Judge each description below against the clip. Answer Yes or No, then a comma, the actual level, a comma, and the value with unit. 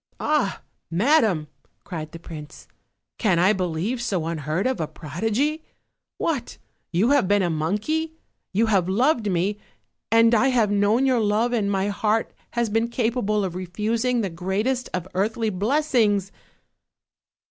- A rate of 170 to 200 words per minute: No, average, 145 wpm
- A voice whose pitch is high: Yes, high, 210 Hz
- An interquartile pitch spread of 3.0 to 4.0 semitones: No, average, 4.6 semitones